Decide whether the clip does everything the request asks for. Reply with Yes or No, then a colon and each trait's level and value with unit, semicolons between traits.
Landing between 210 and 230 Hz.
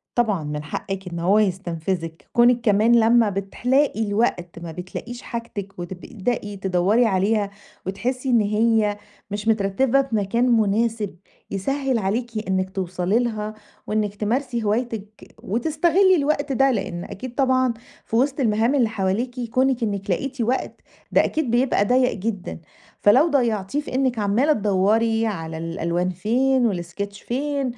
Yes: high, 220 Hz